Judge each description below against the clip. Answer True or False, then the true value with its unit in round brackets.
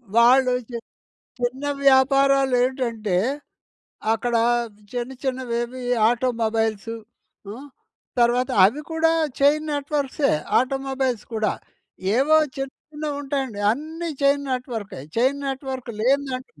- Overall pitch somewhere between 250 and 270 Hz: True (260 Hz)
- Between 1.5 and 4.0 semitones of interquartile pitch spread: True (2.7 semitones)